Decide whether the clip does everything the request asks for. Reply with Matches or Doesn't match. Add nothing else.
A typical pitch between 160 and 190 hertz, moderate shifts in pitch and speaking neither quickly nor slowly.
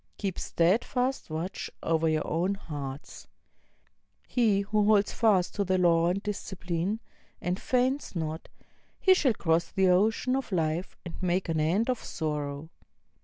Matches